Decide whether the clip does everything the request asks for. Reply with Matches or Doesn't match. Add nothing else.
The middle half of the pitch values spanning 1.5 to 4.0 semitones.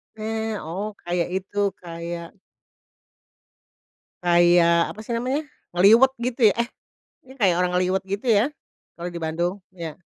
Doesn't match